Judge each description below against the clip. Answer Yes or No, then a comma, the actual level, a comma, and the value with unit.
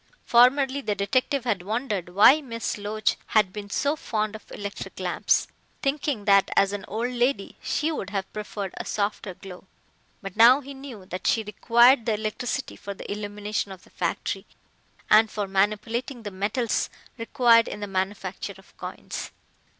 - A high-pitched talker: Yes, high, 215 Hz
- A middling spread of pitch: Yes, average, 3.4 semitones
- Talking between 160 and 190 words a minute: Yes, average, 165 wpm